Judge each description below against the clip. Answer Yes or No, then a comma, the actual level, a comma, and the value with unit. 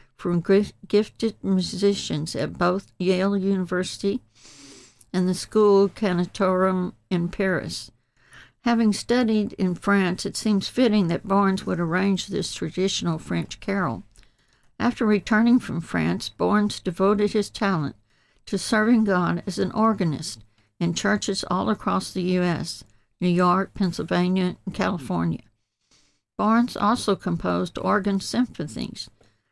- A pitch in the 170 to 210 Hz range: Yes, high, 190 Hz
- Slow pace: Yes, slow, 120 wpm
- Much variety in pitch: No, average, 3.2 semitones